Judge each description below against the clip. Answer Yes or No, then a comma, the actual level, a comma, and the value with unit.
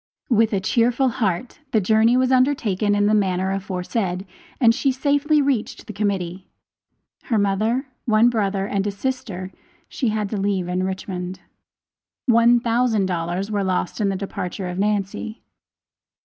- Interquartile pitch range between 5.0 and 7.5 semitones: No, average, 3.7 semitones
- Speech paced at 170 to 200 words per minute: No, average, 150 wpm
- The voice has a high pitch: Yes, high, 205 Hz